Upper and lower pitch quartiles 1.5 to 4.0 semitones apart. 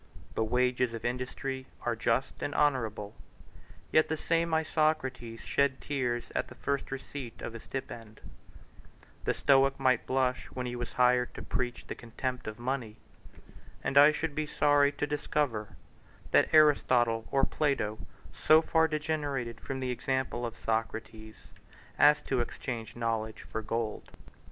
Yes: average, 3.5 semitones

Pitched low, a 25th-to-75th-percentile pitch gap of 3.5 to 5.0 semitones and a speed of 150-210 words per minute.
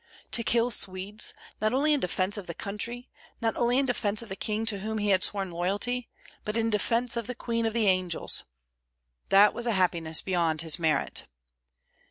No: high, 210 Hz; average, 3.9 semitones; average, 195 wpm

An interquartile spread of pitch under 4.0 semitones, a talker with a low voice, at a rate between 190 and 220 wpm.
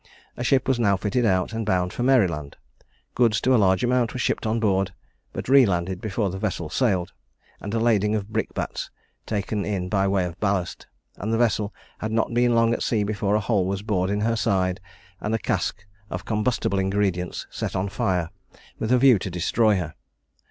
Yes: average, 3.3 semitones; low, 105 Hz; fast, 205 wpm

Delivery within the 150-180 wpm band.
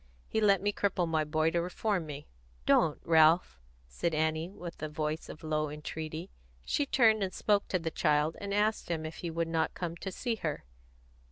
No: average, 195 wpm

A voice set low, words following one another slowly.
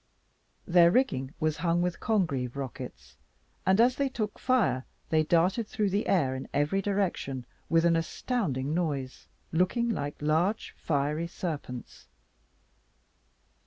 No: medium, 170 Hz; slow, 125 wpm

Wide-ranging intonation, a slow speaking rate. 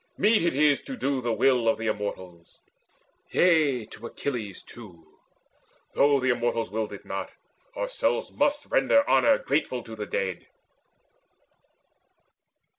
Yes: wide, 6.2 semitones; slow, 130 wpm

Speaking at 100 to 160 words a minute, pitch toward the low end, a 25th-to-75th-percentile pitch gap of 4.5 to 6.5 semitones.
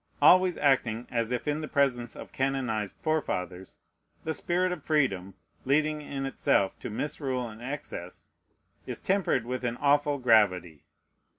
Yes: average, 140 wpm; low, 130 Hz; average, 4.9 semitones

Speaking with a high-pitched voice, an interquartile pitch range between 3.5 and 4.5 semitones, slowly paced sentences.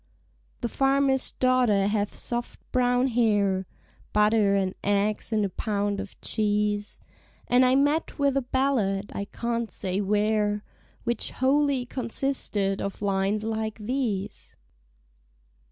Yes: high, 215 Hz; average, 3.8 semitones; slow, 120 wpm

